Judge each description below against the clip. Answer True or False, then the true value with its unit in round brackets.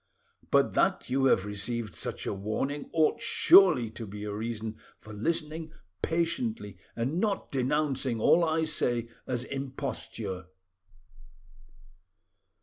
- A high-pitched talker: False (130 Hz)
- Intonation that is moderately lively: False (6.4 semitones)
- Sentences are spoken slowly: True (120 wpm)